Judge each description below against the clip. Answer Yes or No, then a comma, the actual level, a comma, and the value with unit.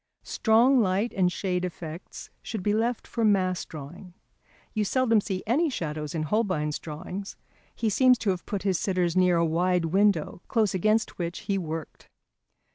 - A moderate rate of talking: Yes, average, 165 wpm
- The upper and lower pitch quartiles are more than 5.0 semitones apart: No, average, 4.1 semitones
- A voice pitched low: No, medium, 185 Hz